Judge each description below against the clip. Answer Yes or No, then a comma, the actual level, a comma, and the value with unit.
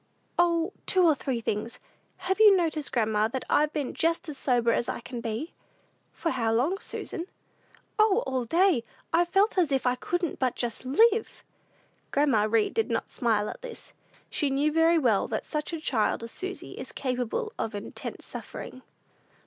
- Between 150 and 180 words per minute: Yes, average, 175 wpm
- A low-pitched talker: No, very high, 290 Hz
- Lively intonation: Yes, wide, 6.6 semitones